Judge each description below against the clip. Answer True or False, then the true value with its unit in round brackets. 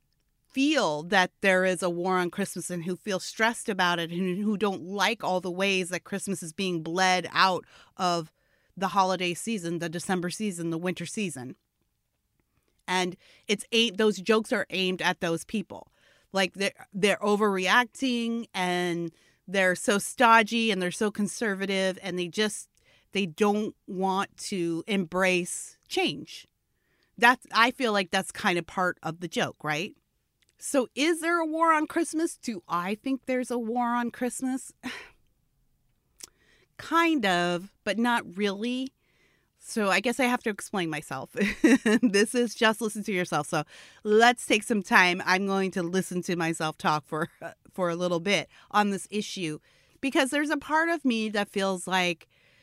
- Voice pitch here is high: True (195 Hz)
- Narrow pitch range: False (4.2 semitones)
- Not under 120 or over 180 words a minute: True (165 wpm)